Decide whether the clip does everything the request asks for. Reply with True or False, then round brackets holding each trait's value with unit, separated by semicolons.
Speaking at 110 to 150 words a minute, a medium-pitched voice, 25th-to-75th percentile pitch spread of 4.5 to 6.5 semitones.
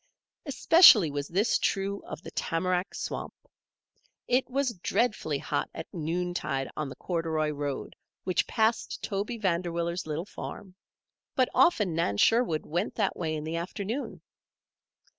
True (135 wpm; 175 Hz; 5.1 semitones)